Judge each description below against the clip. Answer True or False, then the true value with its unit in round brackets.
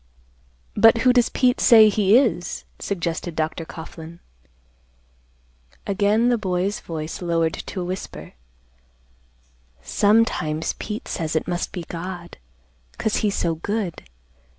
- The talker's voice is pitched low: False (185 Hz)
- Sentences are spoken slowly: True (120 wpm)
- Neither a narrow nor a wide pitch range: True (4.5 semitones)